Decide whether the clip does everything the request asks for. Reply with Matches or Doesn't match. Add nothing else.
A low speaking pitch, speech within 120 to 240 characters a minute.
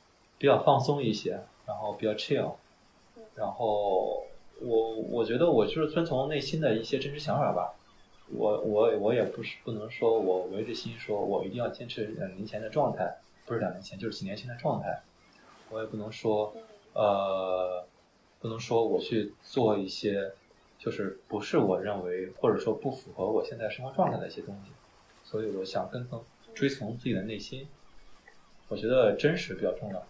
Doesn't match